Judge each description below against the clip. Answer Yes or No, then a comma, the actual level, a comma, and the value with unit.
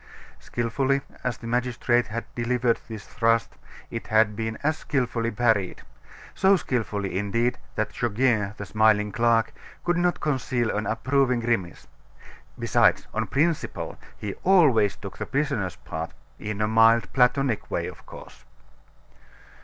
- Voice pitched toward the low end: Yes, low, 115 Hz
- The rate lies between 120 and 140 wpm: Yes, slow, 135 wpm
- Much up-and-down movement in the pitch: No, average, 3.1 semitones